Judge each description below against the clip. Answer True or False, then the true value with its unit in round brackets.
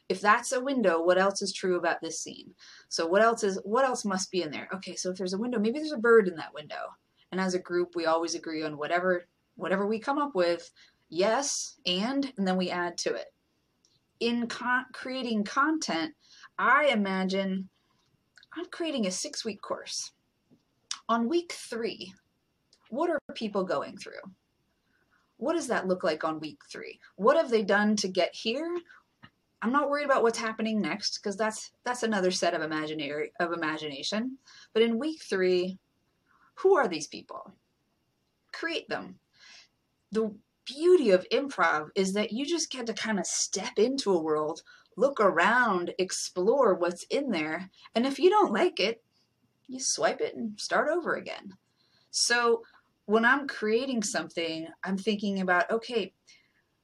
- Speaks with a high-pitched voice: True (215 Hz)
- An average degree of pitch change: False (6.1 semitones)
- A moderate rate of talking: True (170 wpm)